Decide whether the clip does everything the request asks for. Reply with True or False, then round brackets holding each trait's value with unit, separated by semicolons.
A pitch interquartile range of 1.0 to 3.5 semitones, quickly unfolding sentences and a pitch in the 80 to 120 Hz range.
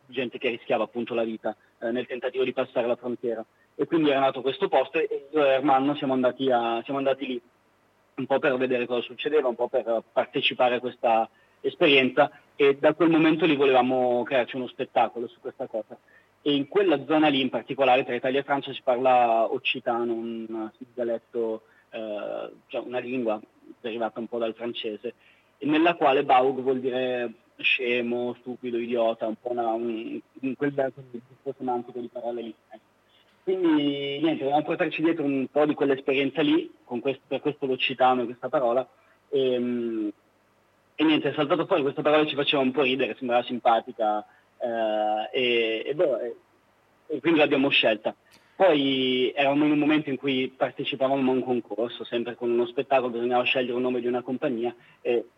False (2.9 semitones; 175 wpm; 130 Hz)